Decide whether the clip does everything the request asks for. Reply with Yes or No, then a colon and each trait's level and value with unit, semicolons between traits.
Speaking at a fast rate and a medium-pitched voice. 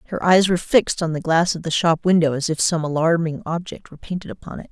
Yes: fast, 255 wpm; medium, 165 Hz